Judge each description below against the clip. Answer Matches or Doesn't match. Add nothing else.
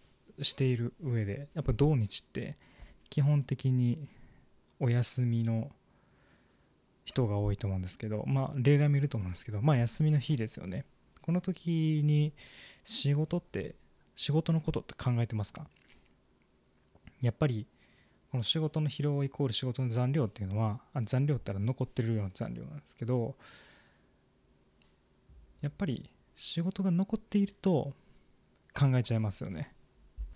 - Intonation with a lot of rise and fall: Doesn't match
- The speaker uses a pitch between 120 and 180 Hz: Matches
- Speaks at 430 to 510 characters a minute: Doesn't match